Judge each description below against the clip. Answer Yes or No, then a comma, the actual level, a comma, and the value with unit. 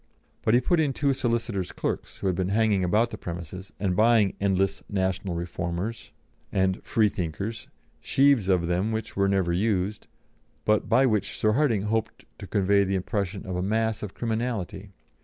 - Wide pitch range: No, average, 3.1 semitones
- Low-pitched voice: Yes, low, 100 Hz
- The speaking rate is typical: Yes, average, 170 wpm